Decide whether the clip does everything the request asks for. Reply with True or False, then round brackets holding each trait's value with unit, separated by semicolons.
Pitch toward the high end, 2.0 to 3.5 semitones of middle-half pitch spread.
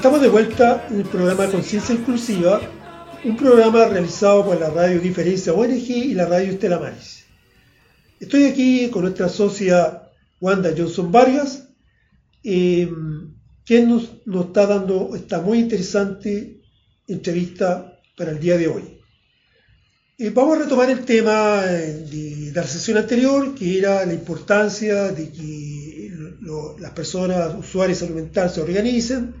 False (195 Hz; 4.7 semitones)